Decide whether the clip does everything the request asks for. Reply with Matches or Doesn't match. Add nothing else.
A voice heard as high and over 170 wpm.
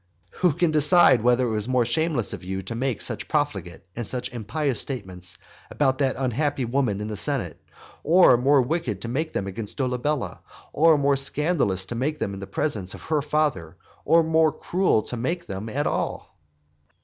Doesn't match